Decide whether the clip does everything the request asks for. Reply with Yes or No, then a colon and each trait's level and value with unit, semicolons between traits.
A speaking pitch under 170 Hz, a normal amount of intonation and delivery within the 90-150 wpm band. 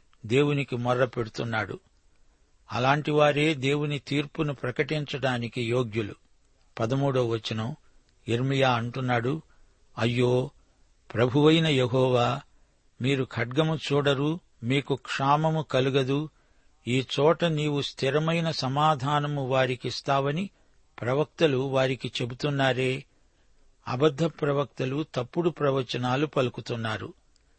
No: low, 135 Hz; average, 3.1 semitones; average, 75 wpm